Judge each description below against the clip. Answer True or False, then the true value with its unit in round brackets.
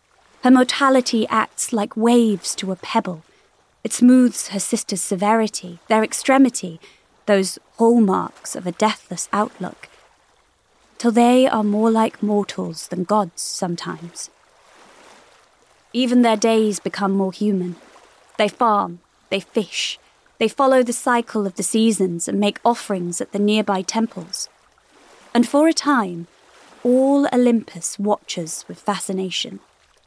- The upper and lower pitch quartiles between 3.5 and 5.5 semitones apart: True (3.8 semitones)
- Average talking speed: False (125 wpm)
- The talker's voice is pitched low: False (215 Hz)